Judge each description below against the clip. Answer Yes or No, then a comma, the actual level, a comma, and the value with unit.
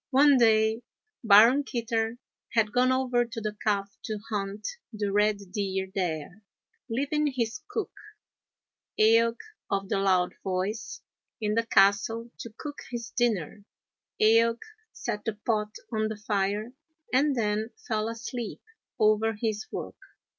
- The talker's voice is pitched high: Yes, high, 220 Hz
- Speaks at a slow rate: Yes, slow, 130 wpm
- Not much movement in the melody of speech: Yes, narrow, 2.3 semitones